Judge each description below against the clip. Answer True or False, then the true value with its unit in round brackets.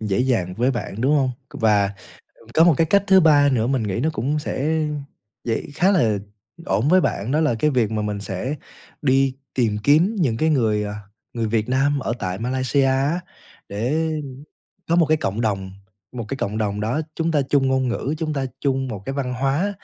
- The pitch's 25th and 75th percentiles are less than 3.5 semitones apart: False (5.2 semitones)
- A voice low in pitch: True (130 Hz)